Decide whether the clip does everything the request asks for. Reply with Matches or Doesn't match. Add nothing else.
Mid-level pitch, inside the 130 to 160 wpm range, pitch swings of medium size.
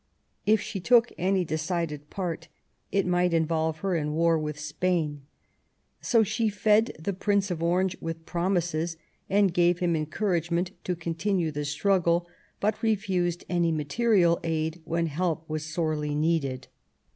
Matches